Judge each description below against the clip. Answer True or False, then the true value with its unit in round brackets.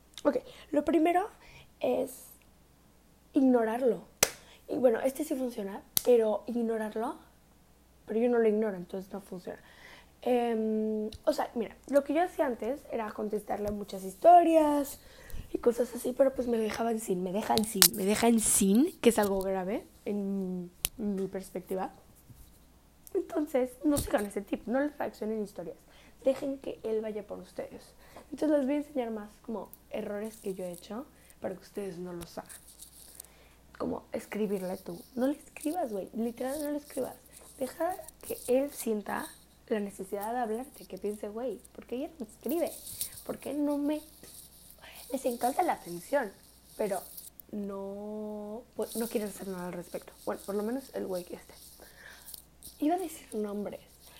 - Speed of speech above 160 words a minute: False (155 wpm)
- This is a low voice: False (230 Hz)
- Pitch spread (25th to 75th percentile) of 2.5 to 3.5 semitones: False (5.2 semitones)